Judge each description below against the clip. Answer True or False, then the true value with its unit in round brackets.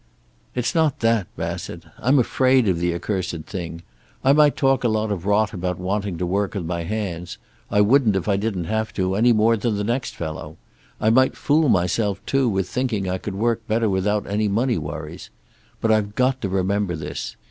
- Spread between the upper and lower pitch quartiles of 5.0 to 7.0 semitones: False (4.1 semitones)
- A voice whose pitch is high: False (105 Hz)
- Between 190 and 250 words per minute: True (200 wpm)